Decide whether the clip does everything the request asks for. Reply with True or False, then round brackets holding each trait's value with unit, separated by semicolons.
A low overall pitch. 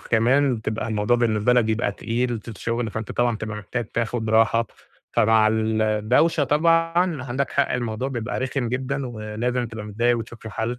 True (115 Hz)